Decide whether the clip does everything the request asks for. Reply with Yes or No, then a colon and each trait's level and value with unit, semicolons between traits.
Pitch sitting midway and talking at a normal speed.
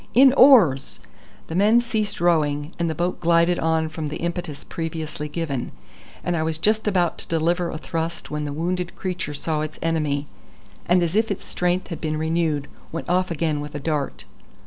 Yes: medium, 165 Hz; average, 185 wpm